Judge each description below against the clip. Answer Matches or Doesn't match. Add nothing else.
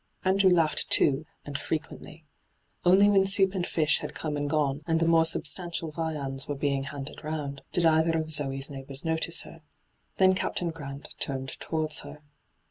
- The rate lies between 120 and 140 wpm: Doesn't match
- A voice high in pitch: Doesn't match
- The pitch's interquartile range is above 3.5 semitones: Doesn't match